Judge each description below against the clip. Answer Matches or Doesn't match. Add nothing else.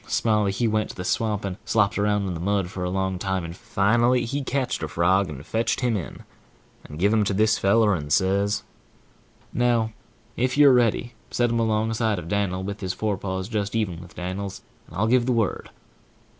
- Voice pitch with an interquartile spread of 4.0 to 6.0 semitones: Doesn't match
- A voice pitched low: Matches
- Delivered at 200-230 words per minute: Matches